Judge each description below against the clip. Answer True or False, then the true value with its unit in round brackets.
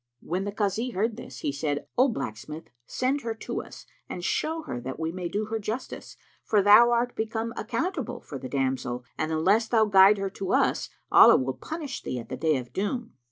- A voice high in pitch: True (205 Hz)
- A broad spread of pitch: True (7.4 semitones)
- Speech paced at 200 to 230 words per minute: True (205 wpm)